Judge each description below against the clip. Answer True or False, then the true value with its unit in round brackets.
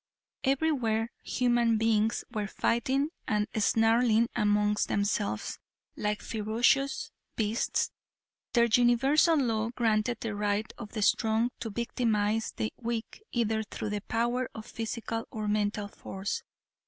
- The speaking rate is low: True (120 wpm)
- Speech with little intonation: True (2.2 semitones)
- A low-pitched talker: False (225 Hz)